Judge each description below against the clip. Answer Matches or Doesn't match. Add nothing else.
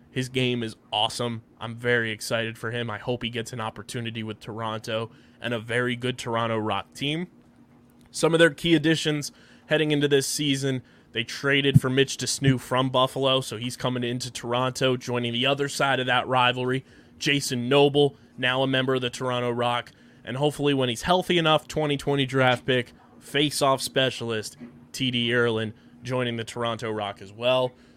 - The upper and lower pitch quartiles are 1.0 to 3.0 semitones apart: Matches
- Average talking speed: Matches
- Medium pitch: Doesn't match